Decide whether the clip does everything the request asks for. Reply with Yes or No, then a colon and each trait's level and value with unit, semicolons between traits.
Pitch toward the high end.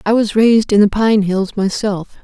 Yes: high, 210 Hz